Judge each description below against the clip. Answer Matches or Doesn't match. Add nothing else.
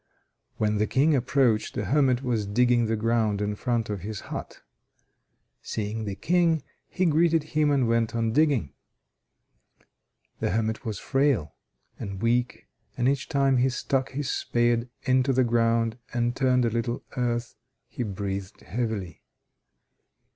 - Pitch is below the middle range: Matches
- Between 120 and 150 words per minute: Matches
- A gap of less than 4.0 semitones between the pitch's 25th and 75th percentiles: Matches